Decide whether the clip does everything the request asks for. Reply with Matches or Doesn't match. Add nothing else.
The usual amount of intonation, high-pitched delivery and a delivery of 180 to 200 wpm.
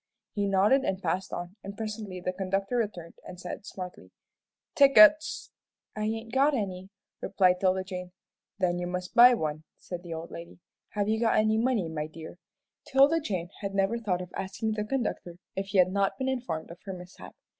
Matches